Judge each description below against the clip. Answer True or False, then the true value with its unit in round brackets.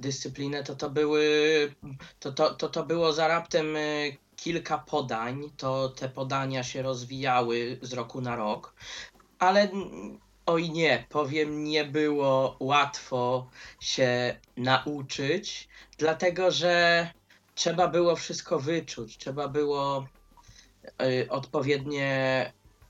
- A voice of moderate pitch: True (145 Hz)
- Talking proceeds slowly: True (105 wpm)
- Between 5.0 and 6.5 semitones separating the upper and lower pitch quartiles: False (3.1 semitones)